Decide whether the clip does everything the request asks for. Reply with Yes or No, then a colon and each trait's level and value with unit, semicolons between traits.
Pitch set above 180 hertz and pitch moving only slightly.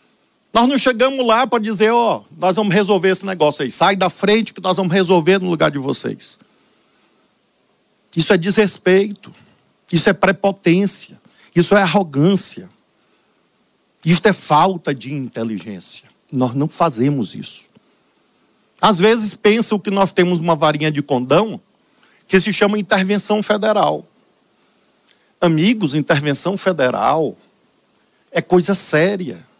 No: high, 190 Hz; average, 3.9 semitones